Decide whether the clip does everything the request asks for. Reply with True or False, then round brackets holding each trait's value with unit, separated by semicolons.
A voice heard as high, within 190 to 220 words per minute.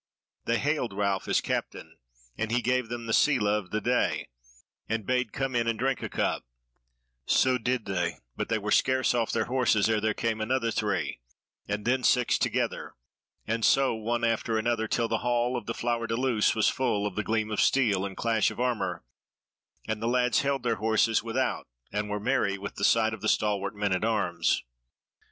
False (115 Hz; 200 wpm)